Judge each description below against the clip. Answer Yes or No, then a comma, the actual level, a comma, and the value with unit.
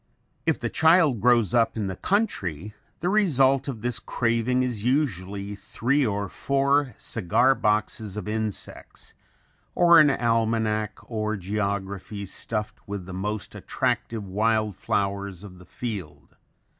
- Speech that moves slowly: Yes, slow, 130 wpm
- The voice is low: Yes, low, 110 Hz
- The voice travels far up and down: No, average, 4.0 semitones